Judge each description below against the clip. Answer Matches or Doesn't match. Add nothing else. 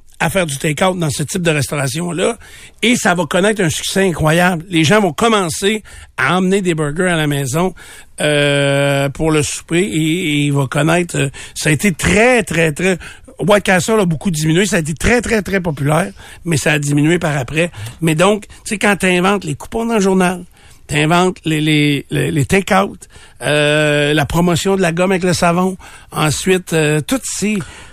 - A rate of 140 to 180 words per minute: Doesn't match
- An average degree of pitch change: Matches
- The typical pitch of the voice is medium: Matches